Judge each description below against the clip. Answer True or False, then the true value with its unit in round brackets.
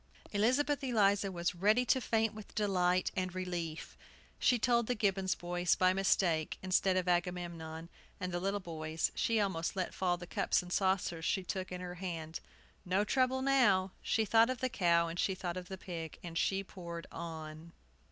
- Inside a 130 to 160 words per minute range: False (180 wpm)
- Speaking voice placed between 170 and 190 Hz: True (185 Hz)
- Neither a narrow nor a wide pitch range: True (3.1 semitones)